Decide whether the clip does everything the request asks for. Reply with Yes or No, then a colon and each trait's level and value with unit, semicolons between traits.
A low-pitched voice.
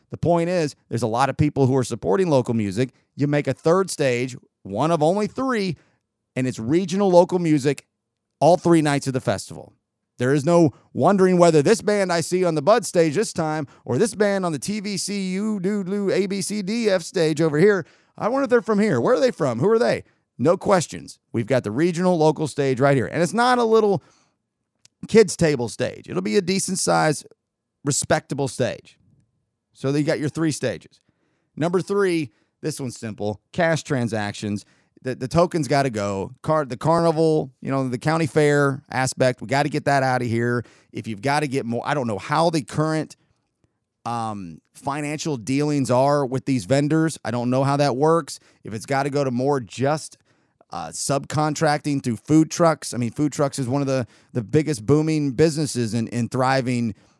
No: medium, 145 Hz